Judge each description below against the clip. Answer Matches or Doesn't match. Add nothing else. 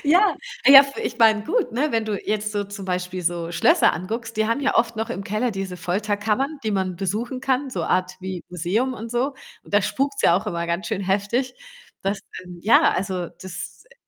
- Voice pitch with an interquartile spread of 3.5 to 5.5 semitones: Matches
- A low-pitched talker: Doesn't match